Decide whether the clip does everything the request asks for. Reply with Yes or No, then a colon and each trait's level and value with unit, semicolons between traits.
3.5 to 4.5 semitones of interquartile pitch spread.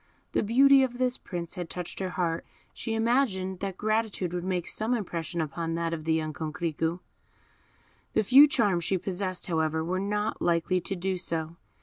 Yes: average, 4.1 semitones